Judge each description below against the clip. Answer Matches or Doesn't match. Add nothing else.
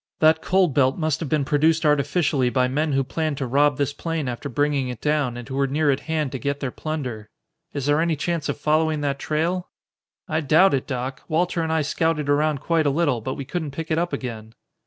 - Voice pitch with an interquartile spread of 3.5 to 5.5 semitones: Doesn't match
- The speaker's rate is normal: Doesn't match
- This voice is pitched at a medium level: Matches